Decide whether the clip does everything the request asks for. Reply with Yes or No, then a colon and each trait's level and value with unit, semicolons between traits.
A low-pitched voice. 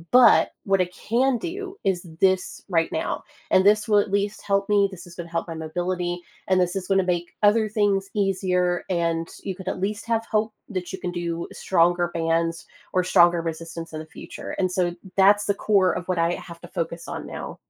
No: medium, 185 Hz